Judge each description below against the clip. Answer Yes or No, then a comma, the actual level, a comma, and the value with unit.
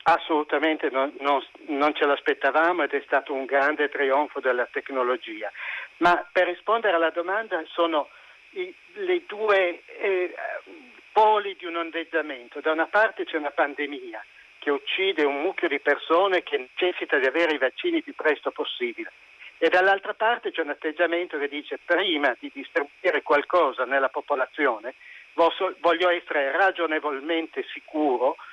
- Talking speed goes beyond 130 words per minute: Yes, average, 140 wpm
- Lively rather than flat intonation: Yes, wide, 6.0 semitones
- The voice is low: No, medium, 170 Hz